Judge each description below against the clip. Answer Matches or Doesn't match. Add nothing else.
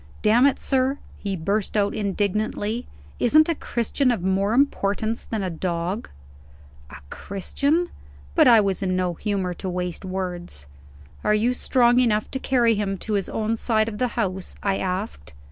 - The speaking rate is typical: Matches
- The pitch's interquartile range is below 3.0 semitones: Doesn't match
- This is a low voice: Doesn't match